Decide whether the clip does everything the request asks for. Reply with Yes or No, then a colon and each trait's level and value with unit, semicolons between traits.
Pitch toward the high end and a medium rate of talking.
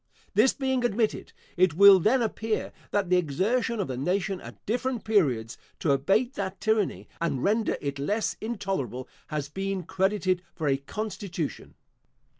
Yes: high, 195 Hz; average, 150 wpm